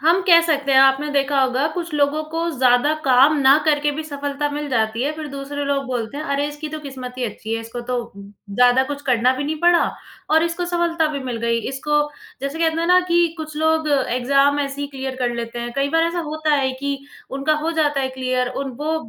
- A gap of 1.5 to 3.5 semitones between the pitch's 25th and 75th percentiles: Yes, average, 3.1 semitones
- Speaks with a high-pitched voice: Yes, very high, 280 Hz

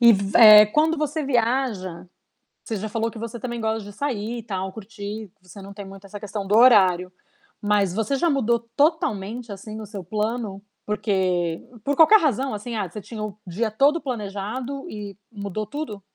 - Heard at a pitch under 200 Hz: No, high, 215 Hz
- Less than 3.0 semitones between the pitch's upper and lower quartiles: No, average, 3.4 semitones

